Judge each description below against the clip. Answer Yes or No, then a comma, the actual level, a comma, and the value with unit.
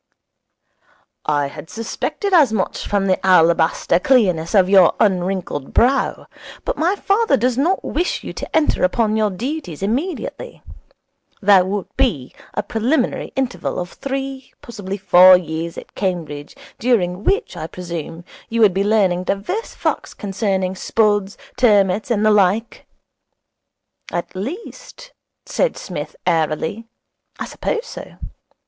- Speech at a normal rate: No, slow, 130 wpm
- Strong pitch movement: Yes, wide, 5.8 semitones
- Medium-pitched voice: No, high, 205 Hz